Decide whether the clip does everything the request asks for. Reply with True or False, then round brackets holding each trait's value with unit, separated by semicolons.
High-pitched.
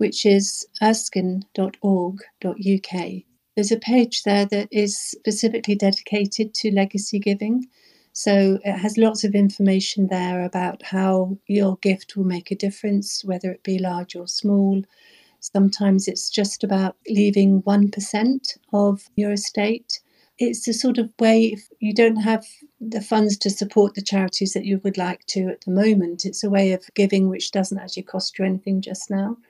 True (200 Hz)